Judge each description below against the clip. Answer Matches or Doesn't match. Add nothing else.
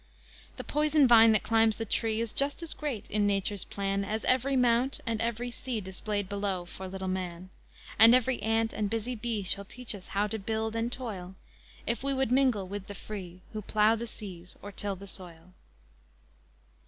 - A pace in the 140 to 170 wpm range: Doesn't match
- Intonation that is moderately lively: Matches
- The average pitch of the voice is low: Doesn't match